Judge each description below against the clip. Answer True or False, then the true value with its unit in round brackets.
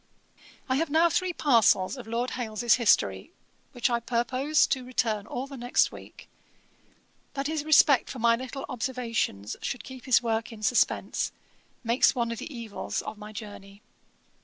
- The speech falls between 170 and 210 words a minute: False (160 wpm)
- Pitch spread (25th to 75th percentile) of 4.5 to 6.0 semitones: False (2.9 semitones)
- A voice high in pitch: True (240 Hz)